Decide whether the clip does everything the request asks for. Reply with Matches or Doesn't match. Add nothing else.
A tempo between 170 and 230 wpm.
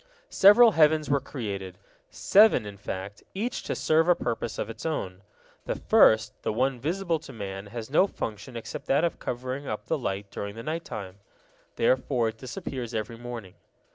Matches